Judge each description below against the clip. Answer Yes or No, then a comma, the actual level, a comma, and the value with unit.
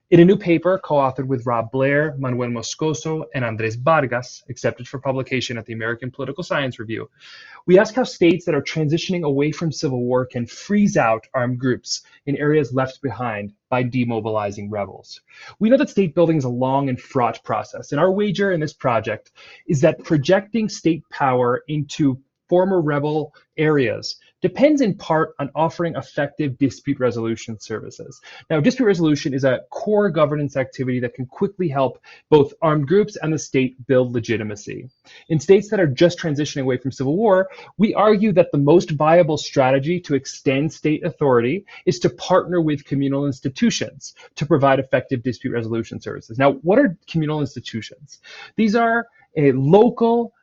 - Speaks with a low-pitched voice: No, medium, 145 Hz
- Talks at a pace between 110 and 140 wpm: No, average, 170 wpm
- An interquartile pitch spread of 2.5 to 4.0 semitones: No, average, 5.2 semitones